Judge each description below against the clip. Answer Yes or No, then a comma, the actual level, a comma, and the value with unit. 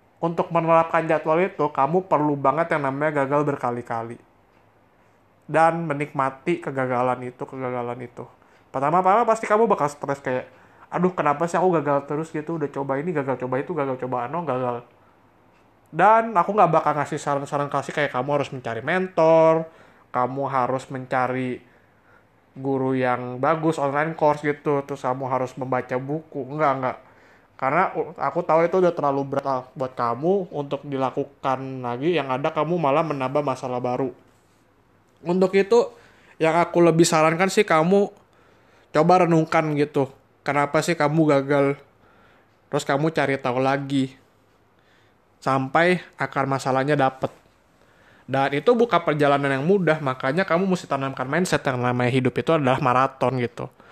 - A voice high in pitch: No, medium, 140 Hz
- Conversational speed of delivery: No, fast, 145 wpm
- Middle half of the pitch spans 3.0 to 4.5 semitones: Yes, average, 3.8 semitones